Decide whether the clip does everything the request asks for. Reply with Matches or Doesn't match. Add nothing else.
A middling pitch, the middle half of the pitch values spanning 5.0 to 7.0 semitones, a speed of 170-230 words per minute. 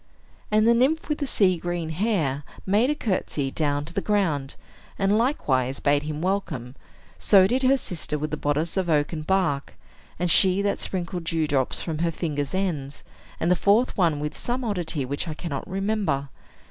Matches